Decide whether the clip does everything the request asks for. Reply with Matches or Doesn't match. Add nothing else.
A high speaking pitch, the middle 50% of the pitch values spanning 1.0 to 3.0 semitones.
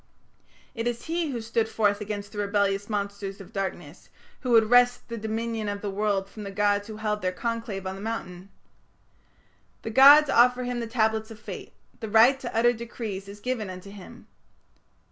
Matches